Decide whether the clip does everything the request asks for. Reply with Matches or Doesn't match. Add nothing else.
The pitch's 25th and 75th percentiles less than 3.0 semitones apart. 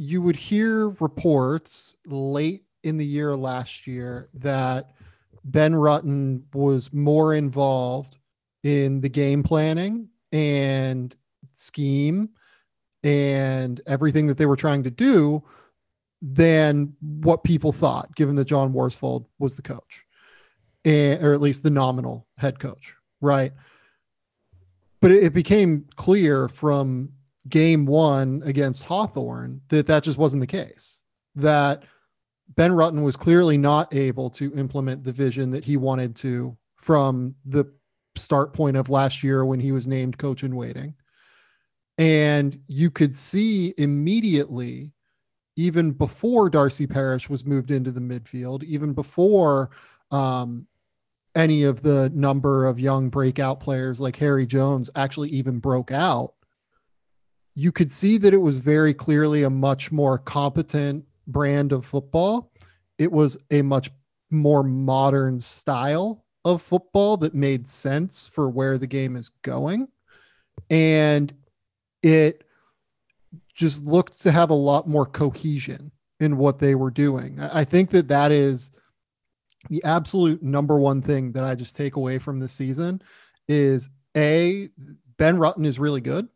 Matches